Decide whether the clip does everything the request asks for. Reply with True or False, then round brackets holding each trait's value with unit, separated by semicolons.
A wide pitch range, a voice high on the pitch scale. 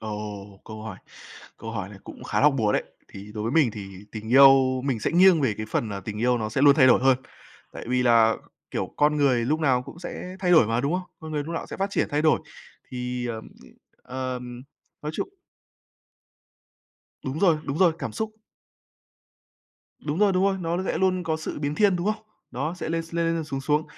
False (6.2 semitones; 135 Hz)